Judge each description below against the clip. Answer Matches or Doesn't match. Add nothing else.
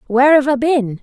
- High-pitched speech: Matches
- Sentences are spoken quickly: Matches